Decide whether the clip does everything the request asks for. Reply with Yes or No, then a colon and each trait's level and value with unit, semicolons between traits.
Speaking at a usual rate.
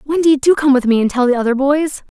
No: fast, 275 wpm